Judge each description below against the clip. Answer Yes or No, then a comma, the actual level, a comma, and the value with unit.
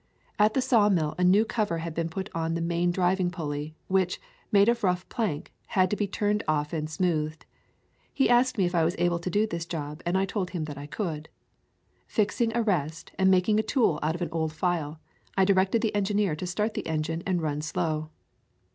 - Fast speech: Yes, fast, 220 wpm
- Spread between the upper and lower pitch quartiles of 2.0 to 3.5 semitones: No, average, 4.3 semitones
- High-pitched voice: No, medium, 175 Hz